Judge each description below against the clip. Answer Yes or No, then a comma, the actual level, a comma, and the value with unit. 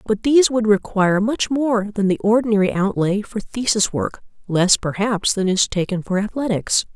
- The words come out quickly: No, average, 175 wpm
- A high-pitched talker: Yes, high, 210 Hz